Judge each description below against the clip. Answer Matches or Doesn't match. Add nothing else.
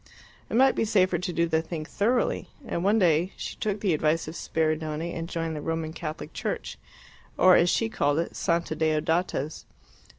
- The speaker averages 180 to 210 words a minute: Matches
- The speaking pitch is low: Doesn't match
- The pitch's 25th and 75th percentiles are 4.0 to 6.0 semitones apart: Doesn't match